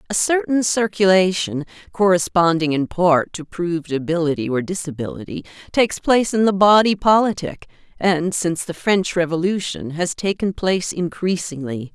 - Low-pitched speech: No, medium, 175 Hz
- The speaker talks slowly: Yes, slow, 130 wpm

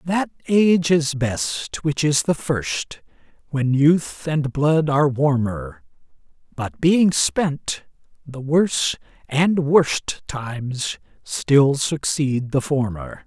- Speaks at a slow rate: Yes, slow, 120 wpm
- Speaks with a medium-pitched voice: Yes, medium, 150 Hz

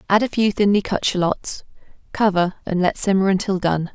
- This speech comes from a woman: Yes, female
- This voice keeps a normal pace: Yes, average, 180 wpm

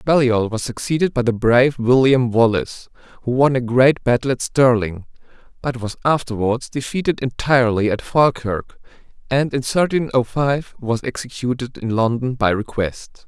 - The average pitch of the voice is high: No, low, 125 Hz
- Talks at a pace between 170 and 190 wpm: No, average, 150 wpm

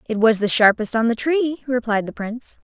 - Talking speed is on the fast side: Yes, fast, 220 wpm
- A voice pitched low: No, high, 235 Hz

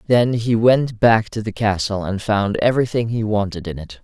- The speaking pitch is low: Yes, low, 110 Hz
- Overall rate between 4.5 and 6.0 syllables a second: Yes, 4.9 syllables/s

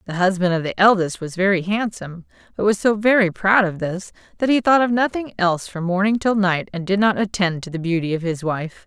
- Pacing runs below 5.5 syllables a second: No, 5.7 syllables/s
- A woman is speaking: Yes, female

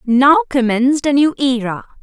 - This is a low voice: No, very high, 265 Hz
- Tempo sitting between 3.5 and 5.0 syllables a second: Yes, 4.7 syllables/s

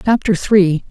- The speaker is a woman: No, male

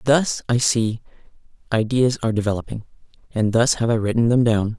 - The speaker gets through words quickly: No, average, 165 wpm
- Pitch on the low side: Yes, low, 115 Hz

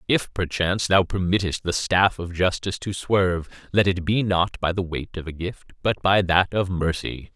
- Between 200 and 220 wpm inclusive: Yes, fast, 205 wpm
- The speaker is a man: Yes, male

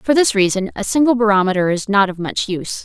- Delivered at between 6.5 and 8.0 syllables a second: No, 6.2 syllables/s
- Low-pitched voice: No, high, 210 Hz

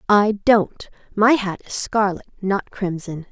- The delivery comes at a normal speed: Yes, average, 145 wpm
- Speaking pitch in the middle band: No, high, 200 Hz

